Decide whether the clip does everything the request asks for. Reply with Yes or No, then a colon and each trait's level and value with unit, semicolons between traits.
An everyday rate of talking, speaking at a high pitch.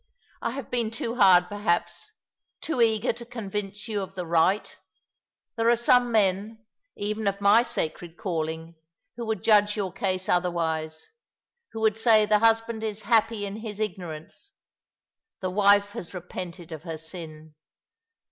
Yes: average, 155 wpm; high, 205 Hz